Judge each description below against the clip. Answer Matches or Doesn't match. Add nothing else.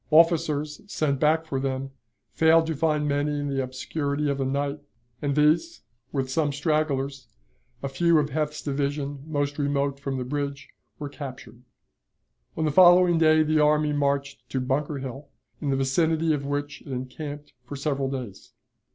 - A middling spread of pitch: Doesn't match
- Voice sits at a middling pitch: Matches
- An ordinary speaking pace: Matches